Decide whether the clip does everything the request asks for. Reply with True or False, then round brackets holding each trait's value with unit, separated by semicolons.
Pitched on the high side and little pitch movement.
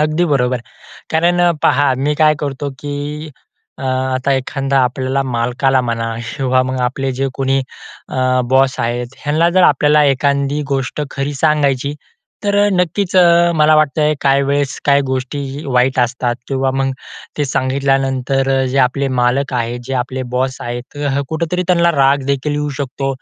False (135 Hz; 2.0 semitones)